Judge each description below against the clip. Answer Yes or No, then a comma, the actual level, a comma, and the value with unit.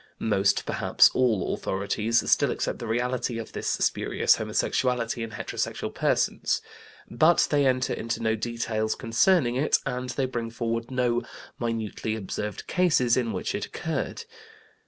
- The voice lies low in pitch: Yes, low, 115 Hz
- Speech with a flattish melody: Yes, narrow, 2.3 semitones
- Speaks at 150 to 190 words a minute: No, average, 140 wpm